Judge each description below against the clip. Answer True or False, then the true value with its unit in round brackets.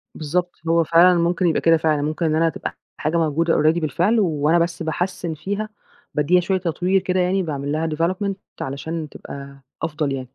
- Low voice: False (165 Hz)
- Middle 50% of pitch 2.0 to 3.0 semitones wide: True (2.7 semitones)